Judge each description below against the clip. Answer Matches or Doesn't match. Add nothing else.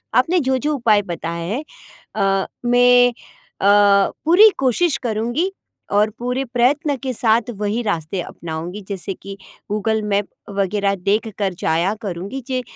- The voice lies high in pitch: Matches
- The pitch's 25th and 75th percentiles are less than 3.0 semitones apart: Doesn't match